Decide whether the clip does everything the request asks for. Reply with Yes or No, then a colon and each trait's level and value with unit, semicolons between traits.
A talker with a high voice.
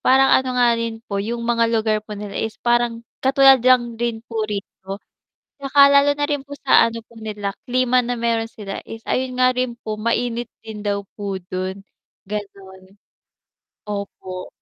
Yes: high, 230 Hz